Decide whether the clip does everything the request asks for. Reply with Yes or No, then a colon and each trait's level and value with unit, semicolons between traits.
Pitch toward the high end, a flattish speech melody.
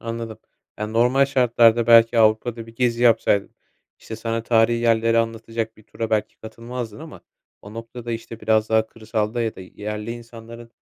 No: low, 115 Hz; narrow, 1.0 semitones